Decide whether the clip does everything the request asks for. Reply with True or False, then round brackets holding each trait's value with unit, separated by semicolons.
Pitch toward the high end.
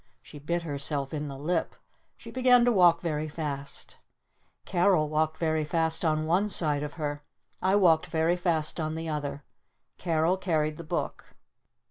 False (160 Hz)